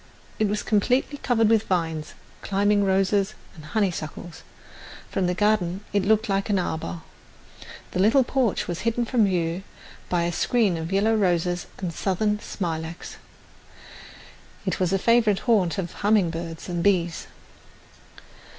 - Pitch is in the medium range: No, high, 195 Hz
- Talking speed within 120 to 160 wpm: Yes, average, 140 wpm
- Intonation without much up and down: No, average, 3.7 semitones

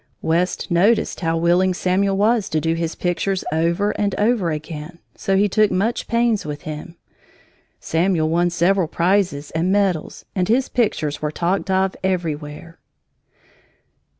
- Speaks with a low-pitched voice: No, medium, 180 Hz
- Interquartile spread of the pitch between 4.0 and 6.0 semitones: No, average, 3.3 semitones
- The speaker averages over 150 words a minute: No, average, 145 wpm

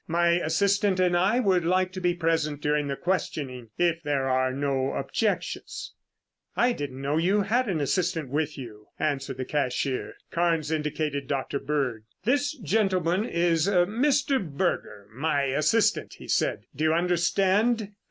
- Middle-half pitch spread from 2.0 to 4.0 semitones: No, average, 5.1 semitones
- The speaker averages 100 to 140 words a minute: No, average, 150 wpm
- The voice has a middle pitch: Yes, medium, 165 Hz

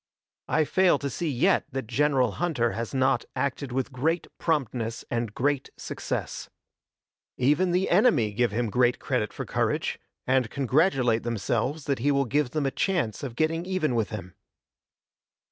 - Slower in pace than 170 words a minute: Yes, average, 160 wpm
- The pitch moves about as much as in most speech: Yes, average, 4.5 semitones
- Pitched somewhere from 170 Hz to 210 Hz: No, low, 135 Hz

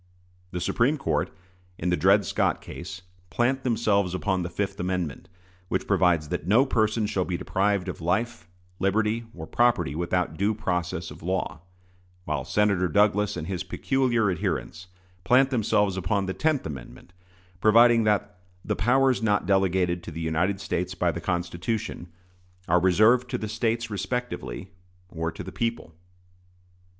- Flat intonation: No, average, 4.0 semitones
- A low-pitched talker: Yes, very low, 95 Hz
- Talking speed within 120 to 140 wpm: No, average, 150 wpm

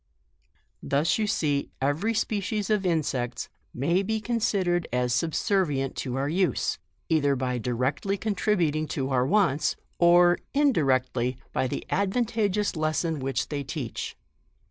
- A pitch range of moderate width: No, wide, 6.8 semitones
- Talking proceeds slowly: Yes, slow, 130 wpm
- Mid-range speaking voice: Yes, medium, 160 Hz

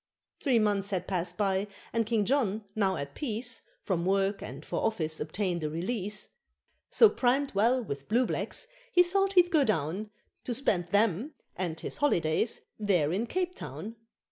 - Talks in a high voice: Yes, high, 210 Hz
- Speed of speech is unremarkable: Yes, average, 170 wpm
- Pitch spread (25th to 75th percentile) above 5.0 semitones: Yes, wide, 5.4 semitones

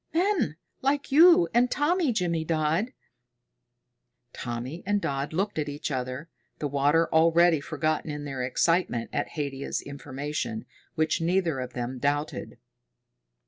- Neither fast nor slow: No, slow, 125 wpm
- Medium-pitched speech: Yes, medium, 155 Hz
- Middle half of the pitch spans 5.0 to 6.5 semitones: Yes, average, 5.3 semitones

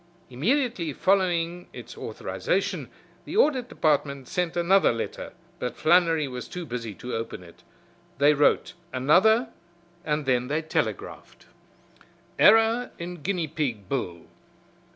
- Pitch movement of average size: No, wide, 6.0 semitones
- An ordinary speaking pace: No, slow, 120 wpm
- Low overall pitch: No, medium, 155 Hz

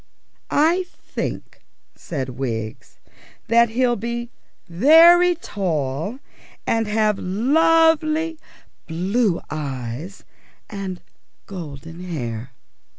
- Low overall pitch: No, high, 200 Hz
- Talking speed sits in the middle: No, slow, 80 wpm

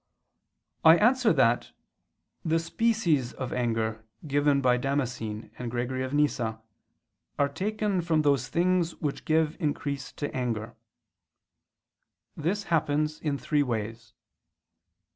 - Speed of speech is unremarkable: No, slow, 120 wpm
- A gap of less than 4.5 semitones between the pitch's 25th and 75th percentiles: No, average, 4.9 semitones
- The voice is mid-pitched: Yes, medium, 145 Hz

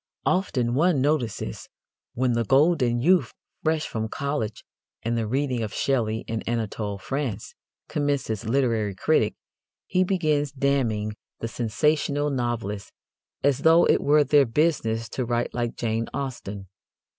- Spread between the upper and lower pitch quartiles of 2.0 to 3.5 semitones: No, average, 4.4 semitones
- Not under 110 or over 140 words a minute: Yes, slow, 135 wpm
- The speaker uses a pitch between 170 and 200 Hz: No, low, 125 Hz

